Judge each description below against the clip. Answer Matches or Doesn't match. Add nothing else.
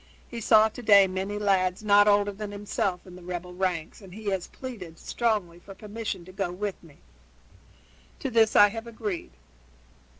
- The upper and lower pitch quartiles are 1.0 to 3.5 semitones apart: Matches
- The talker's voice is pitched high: Matches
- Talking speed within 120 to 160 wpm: Doesn't match